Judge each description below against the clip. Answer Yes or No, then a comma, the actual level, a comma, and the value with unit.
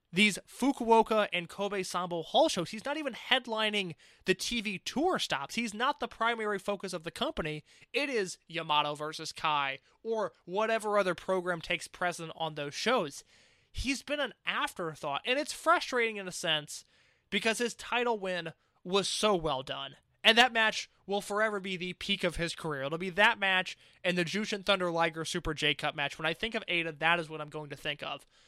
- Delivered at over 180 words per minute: Yes, average, 195 wpm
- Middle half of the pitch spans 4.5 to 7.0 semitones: Yes, wide, 5.4 semitones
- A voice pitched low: No, high, 190 Hz